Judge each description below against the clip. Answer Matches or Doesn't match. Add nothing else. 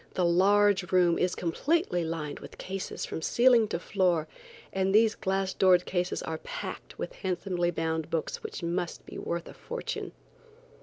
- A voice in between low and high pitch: Matches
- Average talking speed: Matches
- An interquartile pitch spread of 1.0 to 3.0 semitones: Matches